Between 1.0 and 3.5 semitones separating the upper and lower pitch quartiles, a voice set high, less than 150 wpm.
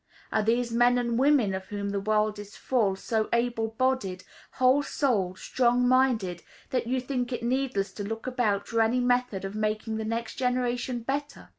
No: average, 2.9 semitones; high, 235 Hz; average, 180 wpm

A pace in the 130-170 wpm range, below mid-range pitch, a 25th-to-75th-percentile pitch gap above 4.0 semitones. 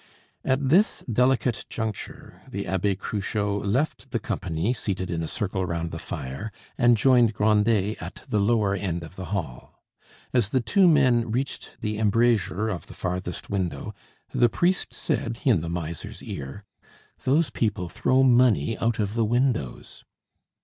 Yes: average, 155 wpm; low, 105 Hz; average, 4.7 semitones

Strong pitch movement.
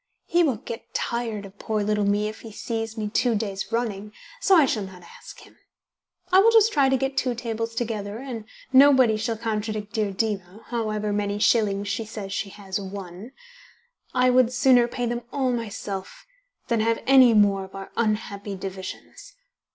No: average, 3.0 semitones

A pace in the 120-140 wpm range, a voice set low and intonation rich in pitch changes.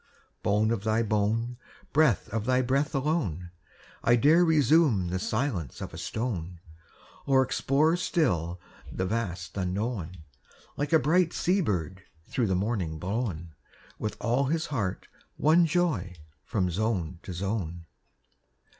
Yes: slow, 135 wpm; low, 110 Hz; wide, 7.3 semitones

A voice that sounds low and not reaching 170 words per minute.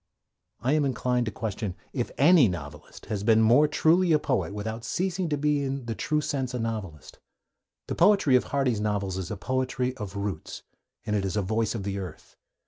No: low, 115 Hz; average, 200 wpm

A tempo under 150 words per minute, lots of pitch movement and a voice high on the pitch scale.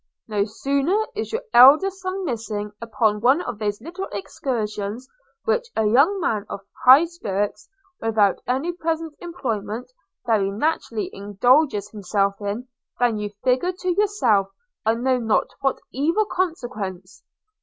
Yes: slow, 135 wpm; wide, 7.9 semitones; high, 245 Hz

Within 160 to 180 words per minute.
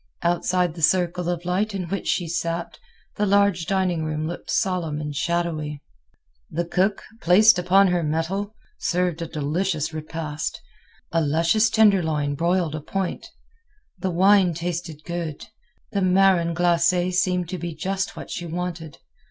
No: average, 145 wpm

